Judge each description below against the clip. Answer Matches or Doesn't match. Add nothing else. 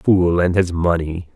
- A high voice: Doesn't match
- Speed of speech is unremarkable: Matches